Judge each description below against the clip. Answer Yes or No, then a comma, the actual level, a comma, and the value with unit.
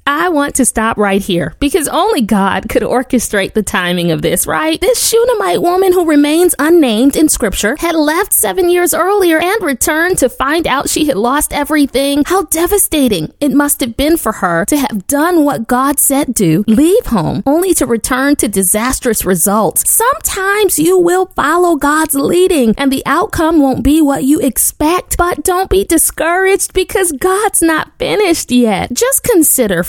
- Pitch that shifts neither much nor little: No, wide, 6.0 semitones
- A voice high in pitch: Yes, very high, 295 Hz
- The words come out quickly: No, average, 170 wpm